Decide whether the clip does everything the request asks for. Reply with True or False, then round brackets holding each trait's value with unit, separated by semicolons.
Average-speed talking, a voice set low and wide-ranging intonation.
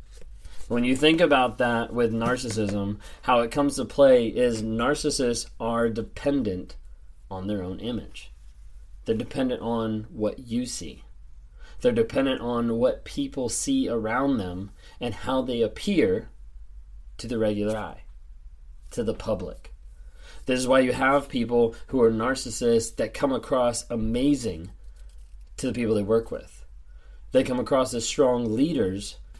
True (145 wpm; 115 Hz; 7.2 semitones)